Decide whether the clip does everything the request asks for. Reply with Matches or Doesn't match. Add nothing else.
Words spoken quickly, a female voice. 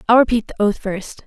Matches